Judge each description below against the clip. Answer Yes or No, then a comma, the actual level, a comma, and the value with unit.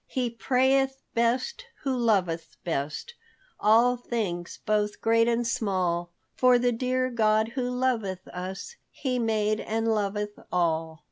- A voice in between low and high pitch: No, high, 225 Hz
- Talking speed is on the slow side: Yes, slow, 130 wpm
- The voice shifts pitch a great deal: No, average, 4.3 semitones